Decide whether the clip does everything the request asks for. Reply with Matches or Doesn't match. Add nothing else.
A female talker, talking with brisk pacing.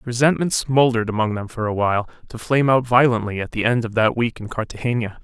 Doesn't match